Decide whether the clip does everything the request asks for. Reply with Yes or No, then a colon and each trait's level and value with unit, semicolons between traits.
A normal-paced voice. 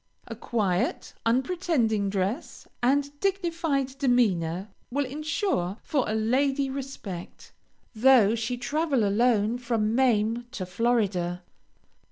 No: slow, 105 wpm